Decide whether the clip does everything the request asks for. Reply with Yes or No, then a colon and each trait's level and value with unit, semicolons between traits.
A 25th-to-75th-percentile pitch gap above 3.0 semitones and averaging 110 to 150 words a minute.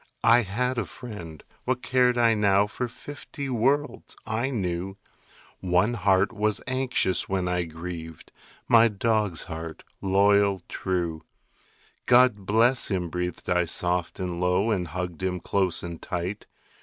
Yes: average, 4.7 semitones; average, 140 wpm